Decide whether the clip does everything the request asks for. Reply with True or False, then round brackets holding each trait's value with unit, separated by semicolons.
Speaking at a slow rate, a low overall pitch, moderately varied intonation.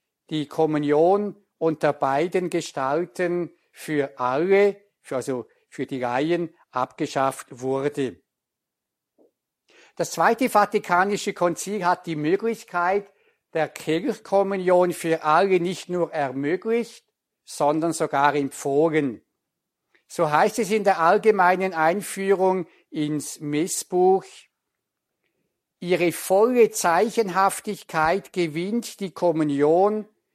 False (90 wpm; 175 Hz; 4.5 semitones)